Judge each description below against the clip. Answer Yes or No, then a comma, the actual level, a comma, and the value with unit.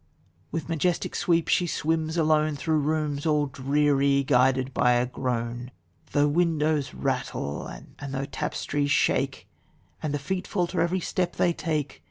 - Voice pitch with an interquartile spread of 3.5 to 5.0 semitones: No, average, 3.1 semitones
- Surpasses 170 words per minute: No, average, 145 wpm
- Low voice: No, medium, 150 Hz